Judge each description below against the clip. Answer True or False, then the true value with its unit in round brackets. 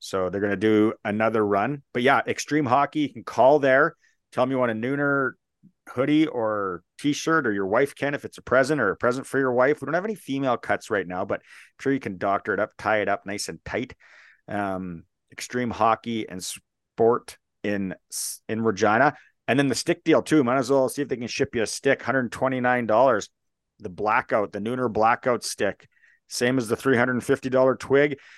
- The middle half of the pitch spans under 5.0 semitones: True (4.2 semitones)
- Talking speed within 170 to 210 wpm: True (205 wpm)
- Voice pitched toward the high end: False (125 Hz)